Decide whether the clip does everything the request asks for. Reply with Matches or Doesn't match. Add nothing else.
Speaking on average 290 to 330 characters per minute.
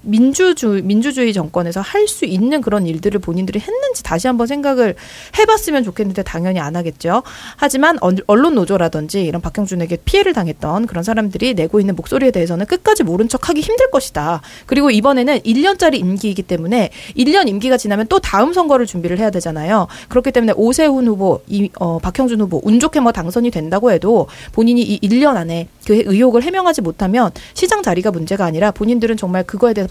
Doesn't match